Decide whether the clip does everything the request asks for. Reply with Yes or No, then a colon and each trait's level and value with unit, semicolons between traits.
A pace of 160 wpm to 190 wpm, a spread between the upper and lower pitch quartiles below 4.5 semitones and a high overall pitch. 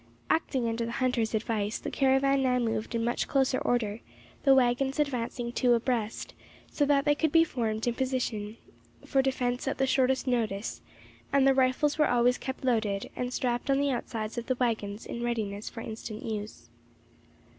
Yes: average, 175 wpm; average, 2.9 semitones; high, 245 Hz